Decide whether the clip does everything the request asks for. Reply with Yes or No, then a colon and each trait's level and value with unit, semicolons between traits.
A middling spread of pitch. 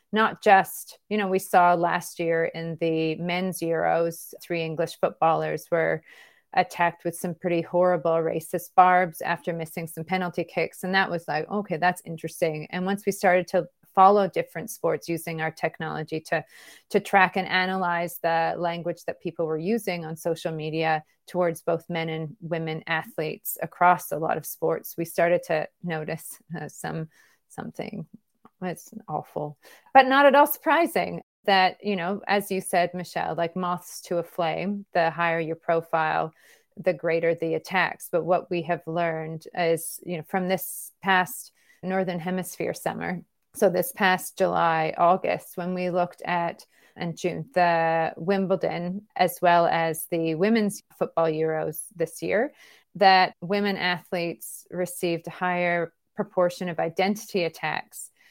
No: narrow, 2.1 semitones